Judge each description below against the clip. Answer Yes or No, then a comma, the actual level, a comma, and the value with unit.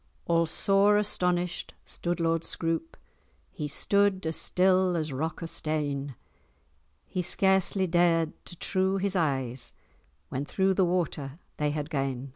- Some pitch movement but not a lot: Yes, average, 4.0 semitones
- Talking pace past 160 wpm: No, slow, 135 wpm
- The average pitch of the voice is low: No, medium, 170 Hz